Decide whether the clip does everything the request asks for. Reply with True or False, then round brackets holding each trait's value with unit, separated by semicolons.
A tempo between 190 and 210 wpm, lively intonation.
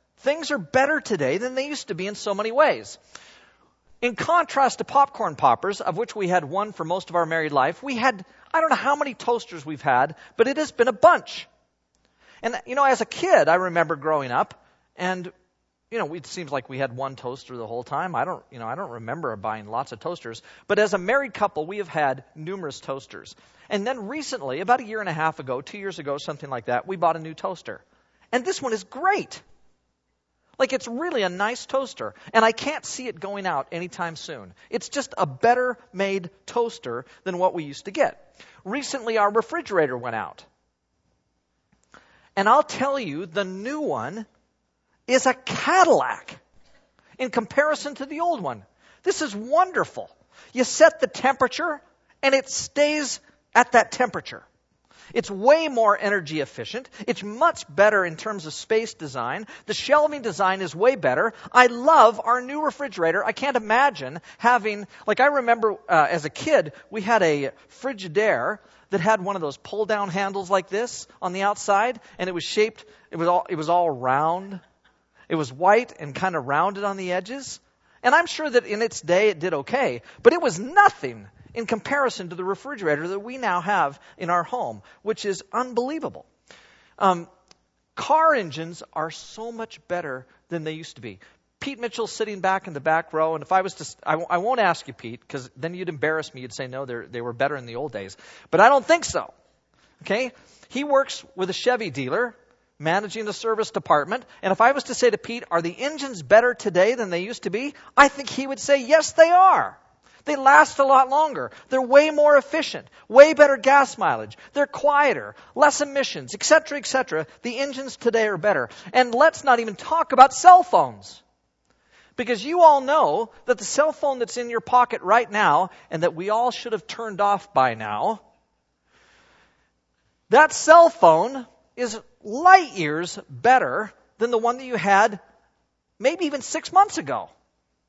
True (195 wpm; 7.7 semitones)